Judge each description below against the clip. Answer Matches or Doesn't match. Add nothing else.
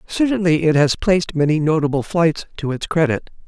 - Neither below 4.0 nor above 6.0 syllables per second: Matches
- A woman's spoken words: Doesn't match